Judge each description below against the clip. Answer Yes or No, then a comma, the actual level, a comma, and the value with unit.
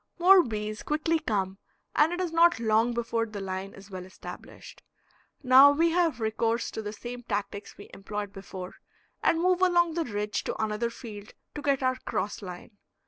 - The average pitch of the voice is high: Yes, high, 230 Hz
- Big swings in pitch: Yes, wide, 6.9 semitones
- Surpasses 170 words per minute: Yes, average, 180 wpm